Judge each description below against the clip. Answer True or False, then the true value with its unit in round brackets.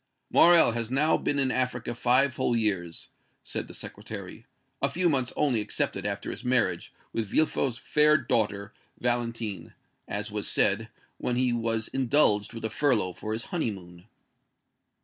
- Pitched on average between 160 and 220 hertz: False (120 Hz)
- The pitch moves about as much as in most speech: True (3.6 semitones)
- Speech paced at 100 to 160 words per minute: True (150 wpm)